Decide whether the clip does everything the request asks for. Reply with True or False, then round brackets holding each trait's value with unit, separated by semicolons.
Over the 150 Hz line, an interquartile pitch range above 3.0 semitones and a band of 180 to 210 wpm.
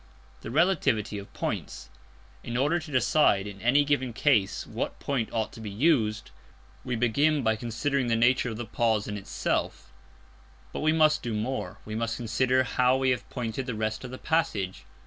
False (120 Hz; 4.0 semitones; 185 wpm)